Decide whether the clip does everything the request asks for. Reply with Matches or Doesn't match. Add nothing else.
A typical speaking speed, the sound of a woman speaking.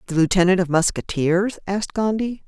Matches